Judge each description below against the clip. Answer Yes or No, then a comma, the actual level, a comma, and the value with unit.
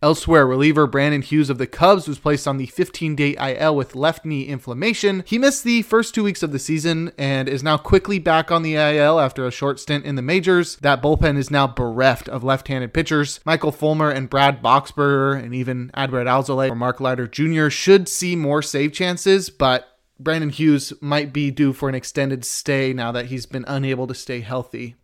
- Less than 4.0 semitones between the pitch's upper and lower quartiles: Yes, average, 3.1 semitones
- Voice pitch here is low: No, medium, 145 Hz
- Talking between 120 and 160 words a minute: No, fast, 205 wpm